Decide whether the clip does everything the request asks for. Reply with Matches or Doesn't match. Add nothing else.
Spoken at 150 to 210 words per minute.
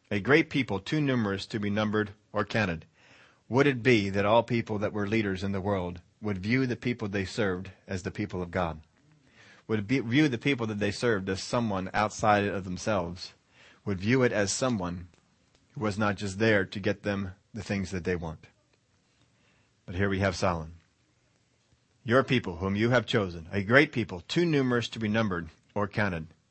Matches